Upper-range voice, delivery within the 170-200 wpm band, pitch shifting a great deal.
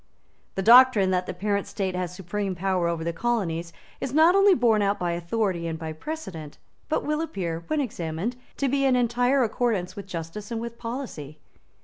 Yes: high, 200 Hz; average, 190 wpm; wide, 6.2 semitones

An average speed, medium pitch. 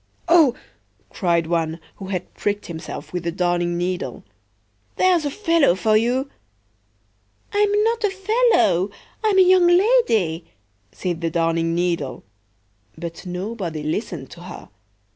No: slow, 125 wpm; medium, 180 Hz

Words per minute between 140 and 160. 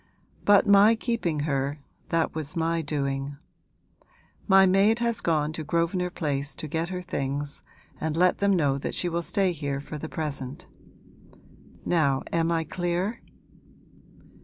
Yes: average, 145 wpm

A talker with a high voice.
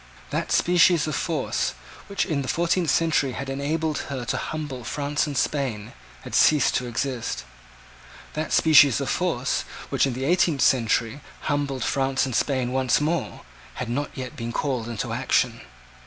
No: medium, 140 Hz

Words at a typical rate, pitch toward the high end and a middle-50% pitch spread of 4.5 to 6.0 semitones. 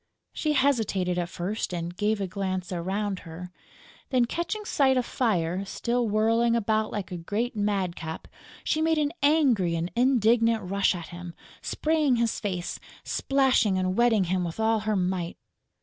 Yes: average, 160 wpm; high, 210 Hz; average, 4.9 semitones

